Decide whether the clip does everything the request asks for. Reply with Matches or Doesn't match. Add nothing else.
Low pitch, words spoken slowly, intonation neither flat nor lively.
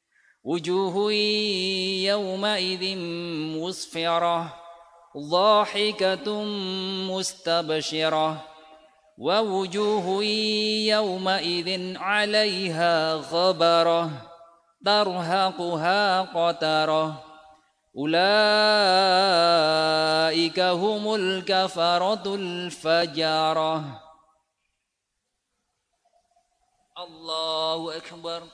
Doesn't match